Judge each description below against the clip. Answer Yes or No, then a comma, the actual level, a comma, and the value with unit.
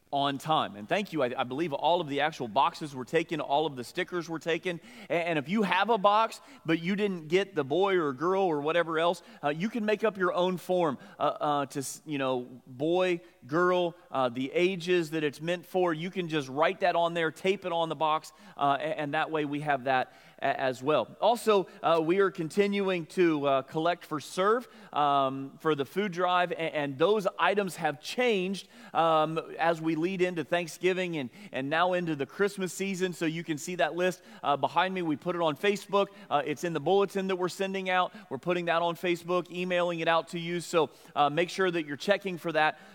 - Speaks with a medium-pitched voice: Yes, medium, 170 Hz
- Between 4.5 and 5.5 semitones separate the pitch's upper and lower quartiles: No, average, 3.3 semitones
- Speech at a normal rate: No, fast, 220 wpm